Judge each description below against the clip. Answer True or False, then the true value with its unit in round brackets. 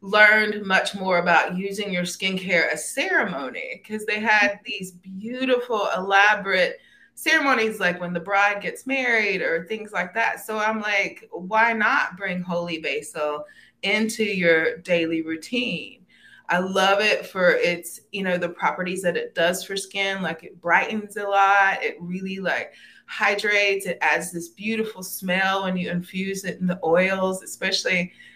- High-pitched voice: True (195 Hz)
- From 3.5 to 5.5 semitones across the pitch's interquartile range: False (3.1 semitones)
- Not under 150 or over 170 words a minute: True (155 wpm)